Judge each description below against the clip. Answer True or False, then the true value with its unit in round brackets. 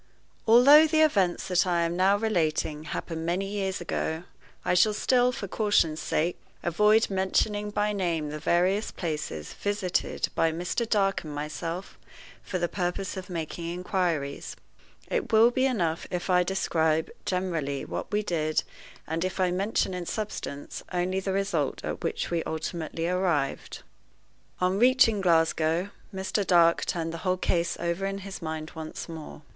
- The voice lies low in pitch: False (180 Hz)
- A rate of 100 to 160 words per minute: True (155 wpm)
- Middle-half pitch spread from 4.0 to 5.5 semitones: False (3.4 semitones)